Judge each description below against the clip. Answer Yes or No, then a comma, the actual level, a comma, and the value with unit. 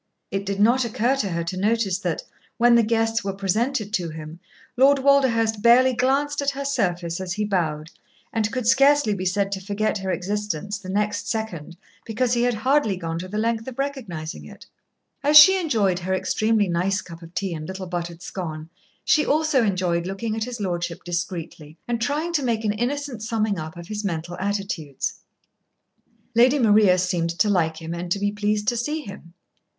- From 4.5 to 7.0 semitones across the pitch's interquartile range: Yes, average, 5.0 semitones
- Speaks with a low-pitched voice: No, high, 205 Hz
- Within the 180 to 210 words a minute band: Yes, average, 190 wpm